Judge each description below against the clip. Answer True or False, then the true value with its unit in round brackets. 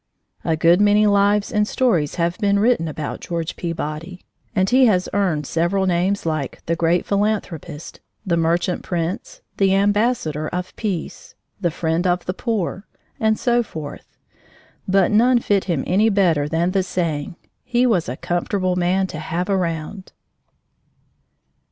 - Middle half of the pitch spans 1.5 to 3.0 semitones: False (3.5 semitones)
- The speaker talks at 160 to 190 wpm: False (150 wpm)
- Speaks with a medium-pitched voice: True (180 Hz)